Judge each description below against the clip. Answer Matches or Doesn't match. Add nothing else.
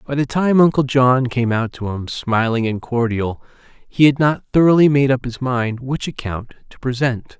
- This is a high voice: Doesn't match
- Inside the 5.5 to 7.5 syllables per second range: Doesn't match